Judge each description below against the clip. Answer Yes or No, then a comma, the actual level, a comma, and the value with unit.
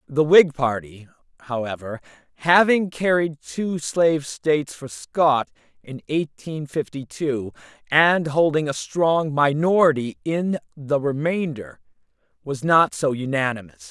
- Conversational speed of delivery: No, slow, 115 wpm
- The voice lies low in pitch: No, medium, 150 Hz